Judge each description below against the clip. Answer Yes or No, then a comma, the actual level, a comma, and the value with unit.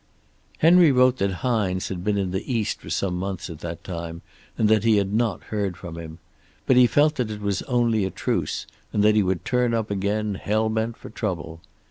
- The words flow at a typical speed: No, fast, 215 wpm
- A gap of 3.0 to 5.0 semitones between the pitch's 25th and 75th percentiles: Yes, average, 3.7 semitones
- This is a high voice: No, low, 105 Hz